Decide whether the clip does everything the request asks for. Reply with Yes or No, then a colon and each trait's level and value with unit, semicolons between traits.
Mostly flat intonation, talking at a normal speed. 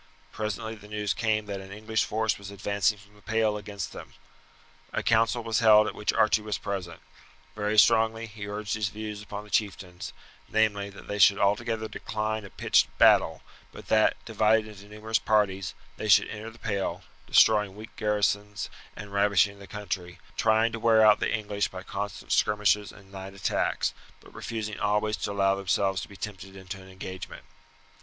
Yes: narrow, 1.5 semitones; average, 180 wpm